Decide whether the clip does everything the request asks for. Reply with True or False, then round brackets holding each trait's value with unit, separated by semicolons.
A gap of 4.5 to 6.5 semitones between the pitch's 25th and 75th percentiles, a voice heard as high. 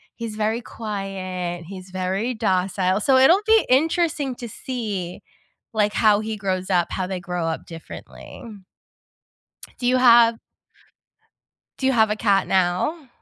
True (4.8 semitones; 210 Hz)